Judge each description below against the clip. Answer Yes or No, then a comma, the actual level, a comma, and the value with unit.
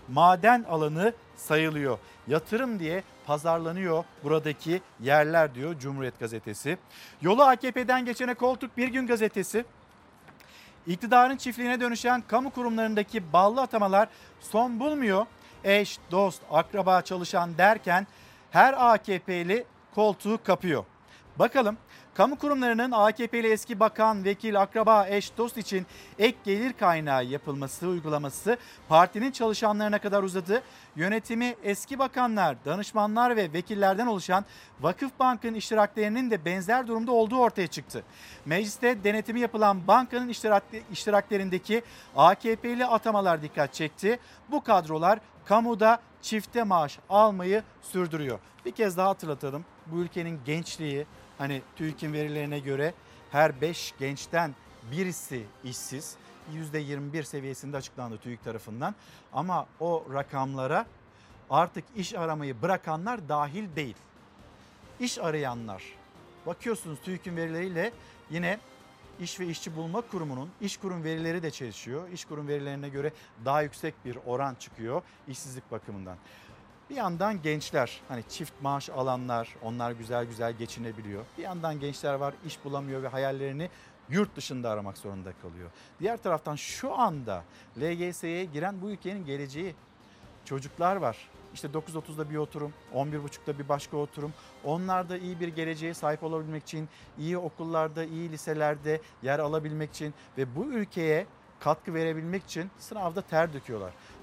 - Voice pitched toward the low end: No, medium, 170 Hz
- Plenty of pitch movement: Yes, wide, 6.6 semitones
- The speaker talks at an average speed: Yes, average, 120 wpm